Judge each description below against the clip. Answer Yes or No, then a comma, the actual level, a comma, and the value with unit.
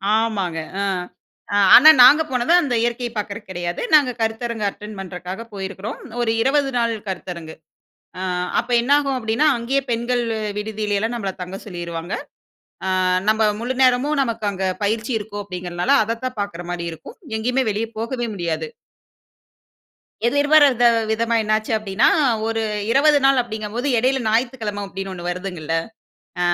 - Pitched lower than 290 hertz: Yes, high, 220 Hz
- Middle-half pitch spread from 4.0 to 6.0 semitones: Yes, average, 4.3 semitones